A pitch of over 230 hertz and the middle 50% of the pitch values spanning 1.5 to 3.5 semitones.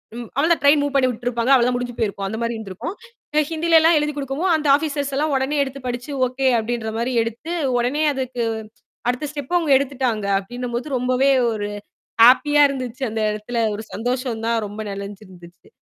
No: very high, 250 Hz; average, 3.9 semitones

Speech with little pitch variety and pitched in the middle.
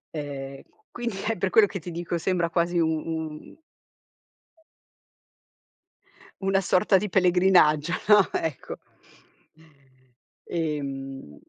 No: average, 3.9 semitones; medium, 170 Hz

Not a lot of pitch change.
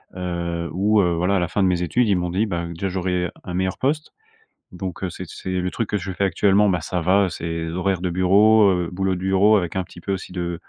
Yes: narrow, 1.9 semitones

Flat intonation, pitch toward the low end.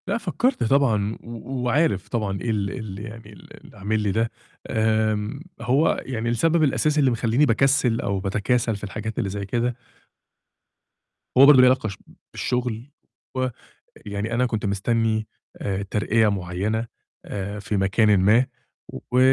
No: average, 3.4 semitones; low, 110 Hz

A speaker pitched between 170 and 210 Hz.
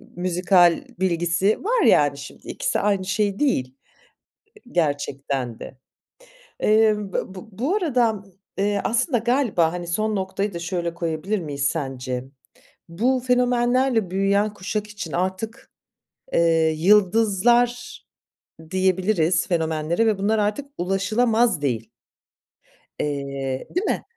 Yes: high, 190 Hz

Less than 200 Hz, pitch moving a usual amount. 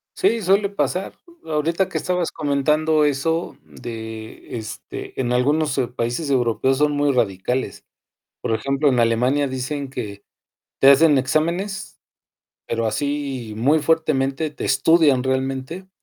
Yes: medium, 140 Hz; average, 4.1 semitones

